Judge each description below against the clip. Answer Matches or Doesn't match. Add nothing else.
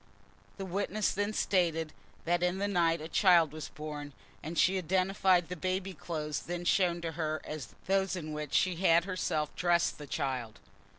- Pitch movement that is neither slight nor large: Matches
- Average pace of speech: Matches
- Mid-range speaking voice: Matches